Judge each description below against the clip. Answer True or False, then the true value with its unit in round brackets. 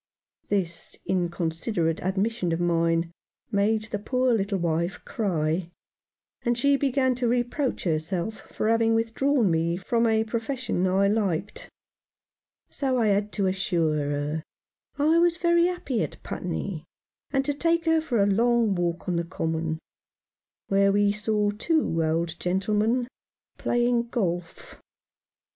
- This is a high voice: True (205 Hz)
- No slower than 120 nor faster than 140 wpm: True (135 wpm)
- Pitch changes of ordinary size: False (5.8 semitones)